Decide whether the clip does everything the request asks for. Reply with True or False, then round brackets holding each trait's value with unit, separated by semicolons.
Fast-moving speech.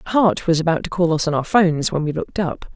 True (285 wpm)